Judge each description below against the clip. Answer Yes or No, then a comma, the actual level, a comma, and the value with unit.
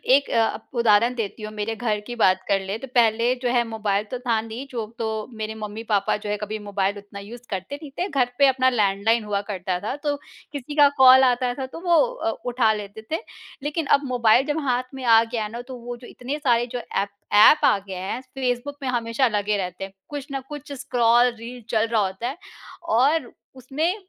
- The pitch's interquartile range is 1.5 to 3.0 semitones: No, average, 3.5 semitones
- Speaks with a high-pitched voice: Yes, high, 235 Hz